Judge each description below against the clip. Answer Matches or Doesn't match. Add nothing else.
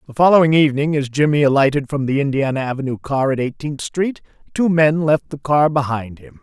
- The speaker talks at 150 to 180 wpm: Doesn't match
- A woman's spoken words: Doesn't match